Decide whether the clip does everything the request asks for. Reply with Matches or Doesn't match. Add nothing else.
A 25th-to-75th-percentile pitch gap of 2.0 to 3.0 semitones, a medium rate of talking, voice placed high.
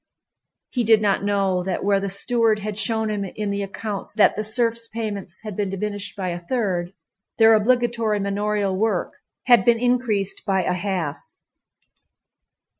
Matches